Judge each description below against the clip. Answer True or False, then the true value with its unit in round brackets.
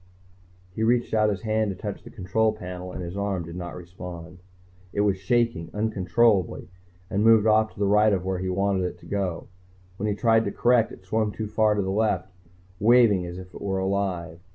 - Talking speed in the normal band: False (210 wpm)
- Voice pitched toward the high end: False (100 Hz)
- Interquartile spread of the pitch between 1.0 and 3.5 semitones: True (3.0 semitones)